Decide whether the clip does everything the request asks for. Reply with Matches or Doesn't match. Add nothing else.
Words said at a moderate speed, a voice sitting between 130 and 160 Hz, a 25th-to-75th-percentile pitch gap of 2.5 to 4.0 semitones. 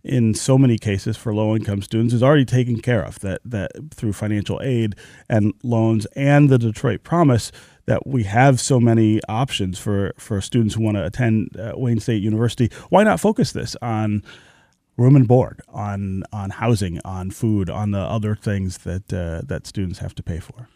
Doesn't match